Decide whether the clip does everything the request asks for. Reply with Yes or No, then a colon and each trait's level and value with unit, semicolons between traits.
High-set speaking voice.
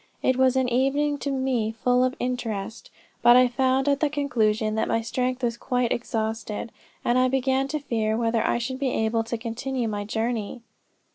Yes: high, 245 Hz